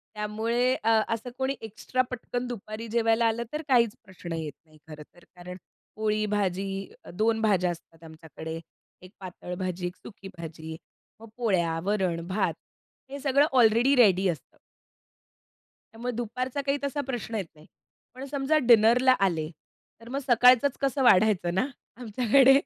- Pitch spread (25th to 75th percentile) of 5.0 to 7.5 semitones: Yes, wide, 5.5 semitones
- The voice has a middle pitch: No, high, 220 Hz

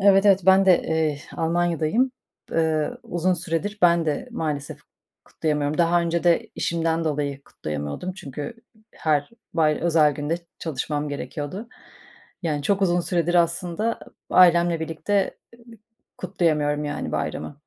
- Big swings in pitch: No, average, 2.9 semitones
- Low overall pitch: No, medium, 165 Hz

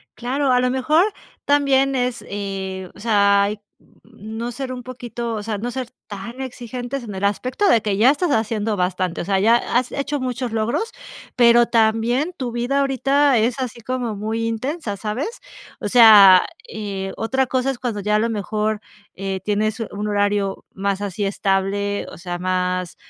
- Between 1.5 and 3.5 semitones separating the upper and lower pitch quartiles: No, average, 3.9 semitones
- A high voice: Yes, high, 225 Hz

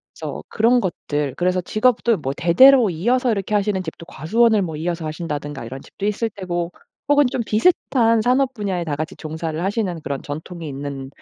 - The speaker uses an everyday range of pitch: No, wide, 6.3 semitones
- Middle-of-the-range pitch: Yes, medium, 180 Hz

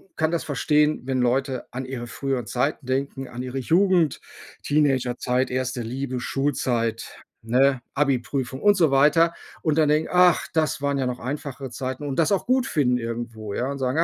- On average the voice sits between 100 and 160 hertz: Yes, low, 135 Hz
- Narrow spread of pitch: No, average, 3.1 semitones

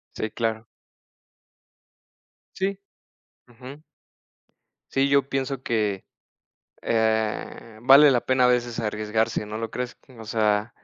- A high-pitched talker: No, low, 115 Hz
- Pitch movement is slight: No, average, 3.2 semitones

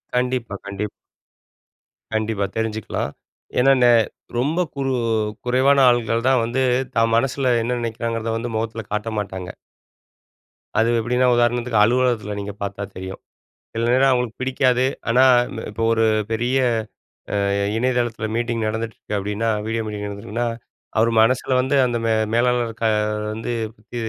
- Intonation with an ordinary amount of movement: No, narrow, 2.2 semitones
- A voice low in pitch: Yes, low, 115 Hz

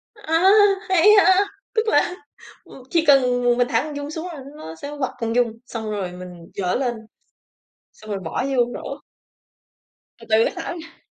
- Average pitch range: No, wide, 6.8 semitones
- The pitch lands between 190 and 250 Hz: No, very high, 260 Hz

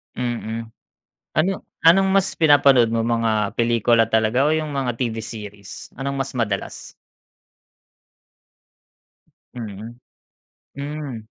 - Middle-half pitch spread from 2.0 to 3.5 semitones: No, average, 4.0 semitones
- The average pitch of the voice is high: No, low, 120 Hz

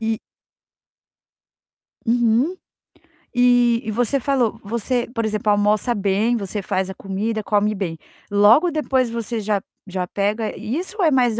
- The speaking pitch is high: Yes, high, 225 Hz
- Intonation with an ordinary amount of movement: Yes, average, 3.0 semitones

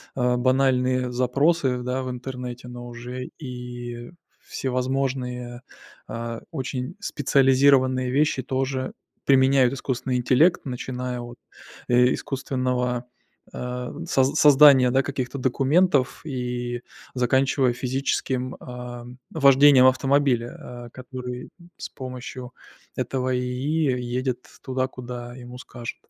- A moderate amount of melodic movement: No, narrow, 1.4 semitones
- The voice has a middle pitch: No, low, 125 Hz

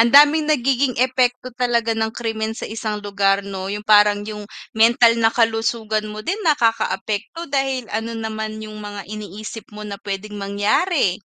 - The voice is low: No, high, 220 Hz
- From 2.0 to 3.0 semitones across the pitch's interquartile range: Yes, narrow, 2.5 semitones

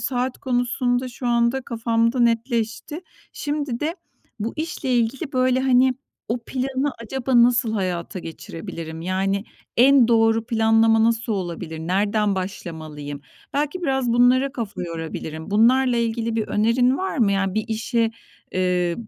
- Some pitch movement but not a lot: Yes, average, 4.3 semitones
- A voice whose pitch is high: Yes, high, 230 Hz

